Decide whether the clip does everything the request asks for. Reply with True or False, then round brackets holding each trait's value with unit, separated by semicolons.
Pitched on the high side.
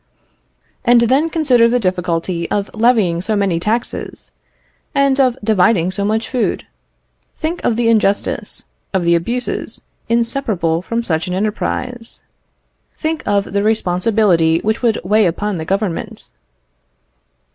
True (215 Hz)